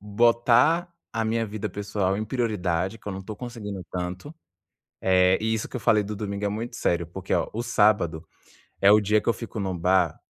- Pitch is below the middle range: Yes, low, 105 Hz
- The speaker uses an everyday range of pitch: Yes, average, 3.2 semitones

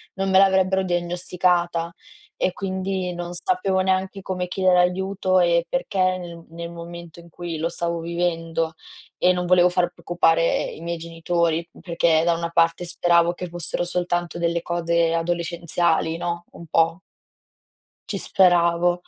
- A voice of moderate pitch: Yes, medium, 175 Hz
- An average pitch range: No, narrow, 1.2 semitones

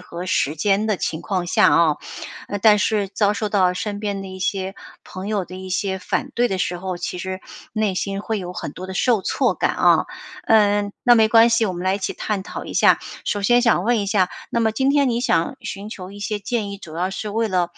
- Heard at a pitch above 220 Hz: No, high, 200 Hz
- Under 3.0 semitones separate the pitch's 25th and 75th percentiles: Yes, narrow, 2.6 semitones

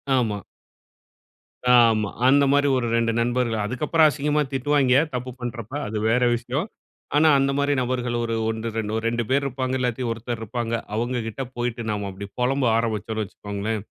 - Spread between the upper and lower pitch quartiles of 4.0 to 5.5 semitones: No, average, 2.7 semitones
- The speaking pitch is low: Yes, low, 120 Hz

